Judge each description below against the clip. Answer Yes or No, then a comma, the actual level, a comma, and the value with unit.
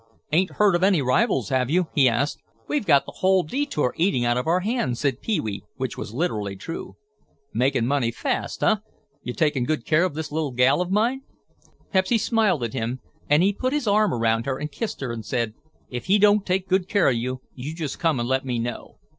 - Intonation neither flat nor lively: No, wide, 7.2 semitones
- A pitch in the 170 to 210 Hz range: No, medium, 150 Hz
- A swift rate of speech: Yes, fast, 220 wpm